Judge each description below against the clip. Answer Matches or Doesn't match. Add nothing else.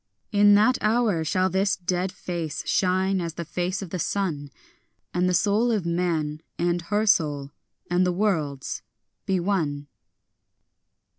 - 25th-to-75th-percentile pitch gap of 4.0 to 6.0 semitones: Doesn't match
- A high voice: Doesn't match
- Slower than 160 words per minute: Matches